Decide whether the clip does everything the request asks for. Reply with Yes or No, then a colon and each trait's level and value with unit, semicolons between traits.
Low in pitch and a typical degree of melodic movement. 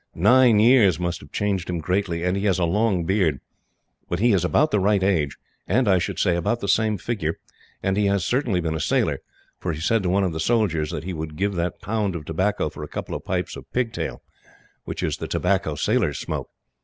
Yes: very low, 95 Hz; average, 3.8 semitones